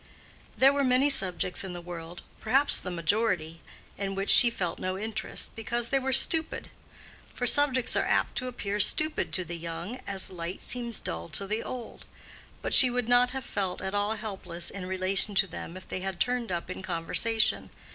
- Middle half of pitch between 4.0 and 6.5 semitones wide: Yes, average, 5.1 semitones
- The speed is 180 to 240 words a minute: Yes, average, 185 wpm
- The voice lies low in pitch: No, high, 200 Hz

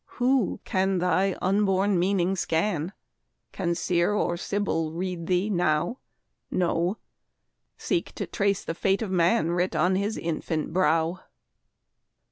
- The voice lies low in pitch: No, medium, 185 Hz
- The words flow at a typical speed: No, slow, 125 wpm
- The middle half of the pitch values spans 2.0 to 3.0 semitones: Yes, narrow, 2.5 semitones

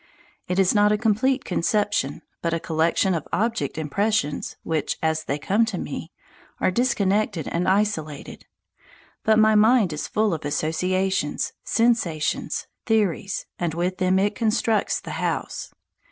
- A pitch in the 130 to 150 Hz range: No, high, 190 Hz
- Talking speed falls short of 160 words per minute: Yes, average, 140 wpm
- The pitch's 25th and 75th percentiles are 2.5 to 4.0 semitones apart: No, average, 4.9 semitones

